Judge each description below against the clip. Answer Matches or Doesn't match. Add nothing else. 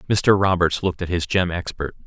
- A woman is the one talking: Doesn't match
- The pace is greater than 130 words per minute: Matches